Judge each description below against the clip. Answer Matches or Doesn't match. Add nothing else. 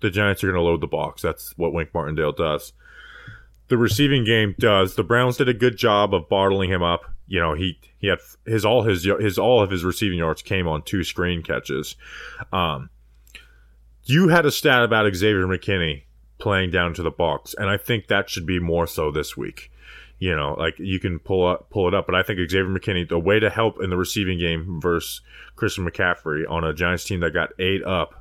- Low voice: Matches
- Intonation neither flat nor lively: Matches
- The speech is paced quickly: Matches